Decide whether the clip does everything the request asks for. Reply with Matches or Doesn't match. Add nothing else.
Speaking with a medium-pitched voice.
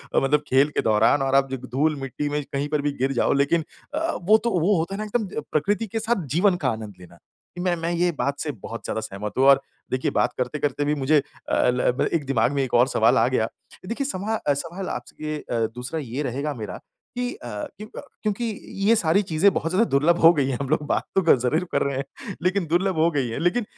Matches